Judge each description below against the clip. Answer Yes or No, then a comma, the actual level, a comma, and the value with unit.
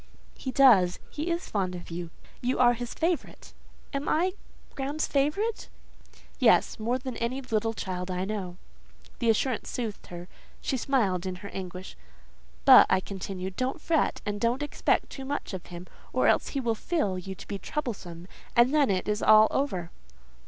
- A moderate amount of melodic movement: No, wide, 6.4 semitones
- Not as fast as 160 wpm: No, average, 175 wpm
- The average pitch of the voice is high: Yes, high, 225 Hz